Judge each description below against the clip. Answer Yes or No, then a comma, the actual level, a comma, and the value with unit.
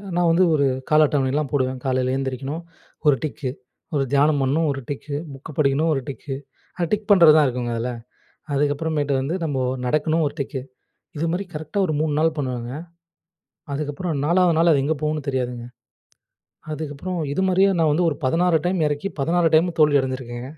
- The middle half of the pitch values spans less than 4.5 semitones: Yes, average, 3.2 semitones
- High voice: No, medium, 150 Hz